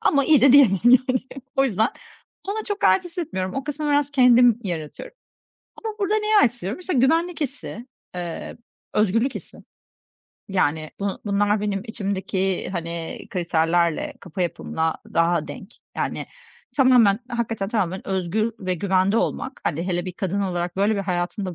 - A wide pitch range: Yes, wide, 6.2 semitones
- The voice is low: No, high, 205 Hz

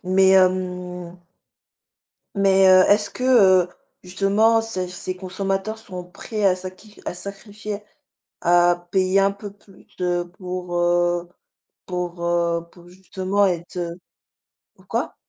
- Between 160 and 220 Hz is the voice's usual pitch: Yes, medium, 185 Hz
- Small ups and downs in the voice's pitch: Yes, narrow, 1.9 semitones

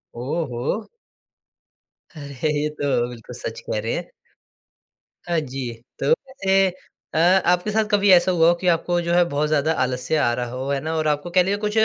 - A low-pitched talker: No, medium, 160 Hz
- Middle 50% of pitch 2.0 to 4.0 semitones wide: No, average, 4.6 semitones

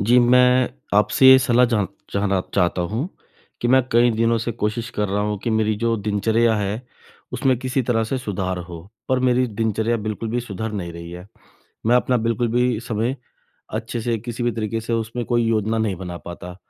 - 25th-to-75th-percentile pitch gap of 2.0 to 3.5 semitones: Yes, average, 2.7 semitones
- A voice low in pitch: Yes, low, 115 Hz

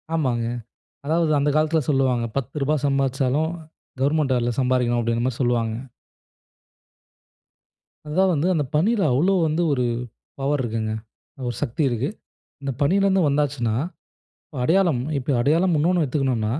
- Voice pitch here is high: No, medium, 140 Hz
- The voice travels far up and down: No, average, 4.2 semitones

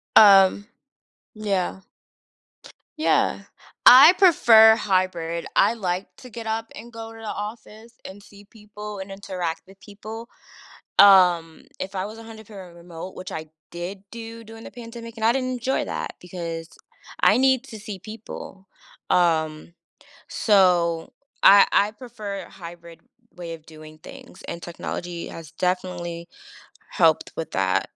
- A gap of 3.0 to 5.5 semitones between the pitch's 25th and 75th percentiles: Yes, average, 4.3 semitones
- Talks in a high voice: Yes, high, 200 Hz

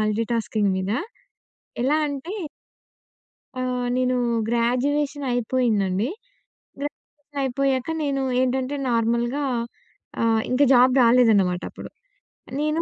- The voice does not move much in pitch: No, average, 3.2 semitones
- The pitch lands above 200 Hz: Yes, very high, 250 Hz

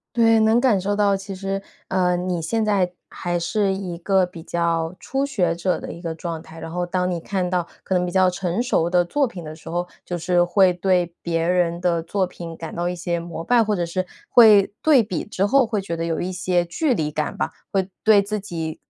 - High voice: No, medium, 180 Hz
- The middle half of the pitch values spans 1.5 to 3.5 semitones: Yes, average, 2.7 semitones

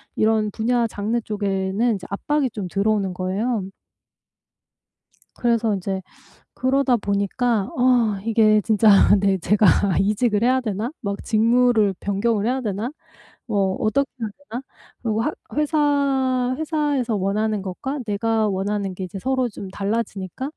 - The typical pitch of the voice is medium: No, high, 220 Hz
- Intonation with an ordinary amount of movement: Yes, average, 3.7 semitones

